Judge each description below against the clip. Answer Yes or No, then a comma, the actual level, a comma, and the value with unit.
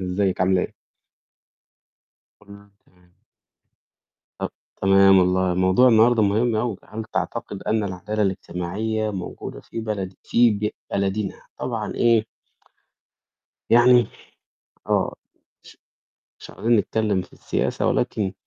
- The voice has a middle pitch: No, low, 100 Hz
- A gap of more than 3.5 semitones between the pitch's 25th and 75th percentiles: No, average, 2.9 semitones